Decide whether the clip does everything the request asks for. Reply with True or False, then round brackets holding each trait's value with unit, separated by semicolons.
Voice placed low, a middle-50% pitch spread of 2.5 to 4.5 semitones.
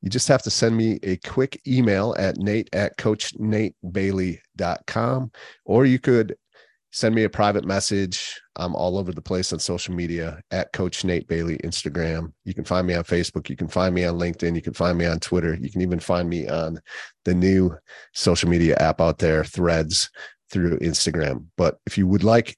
True (90 Hz; 3.5 semitones)